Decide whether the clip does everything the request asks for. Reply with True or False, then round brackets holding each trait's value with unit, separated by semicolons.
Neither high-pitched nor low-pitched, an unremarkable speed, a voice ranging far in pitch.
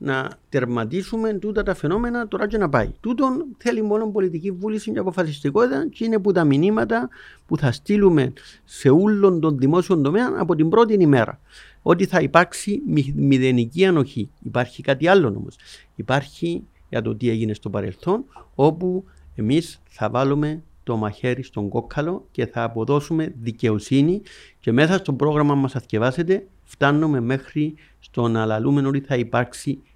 True (150 Hz; 150 wpm; 7.3 semitones)